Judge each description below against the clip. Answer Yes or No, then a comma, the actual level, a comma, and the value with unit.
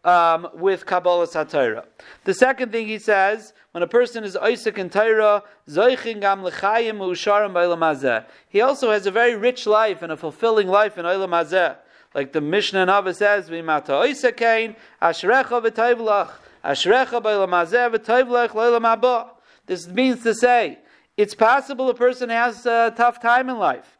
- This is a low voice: No, high, 215 Hz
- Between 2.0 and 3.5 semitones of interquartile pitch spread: No, average, 4.4 semitones